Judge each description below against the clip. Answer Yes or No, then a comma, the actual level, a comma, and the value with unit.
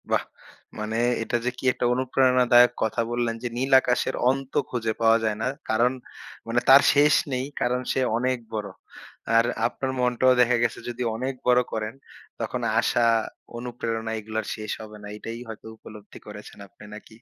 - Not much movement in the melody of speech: Yes, narrow, 2.2 semitones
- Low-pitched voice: Yes, low, 120 Hz